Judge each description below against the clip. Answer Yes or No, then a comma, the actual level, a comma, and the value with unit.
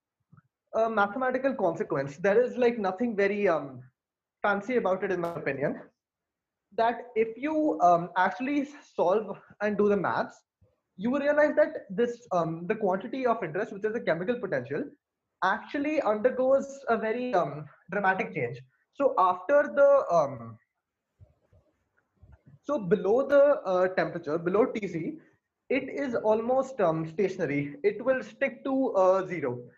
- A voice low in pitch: No, high, 210 Hz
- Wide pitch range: Yes, wide, 6.5 semitones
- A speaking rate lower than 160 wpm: Yes, average, 140 wpm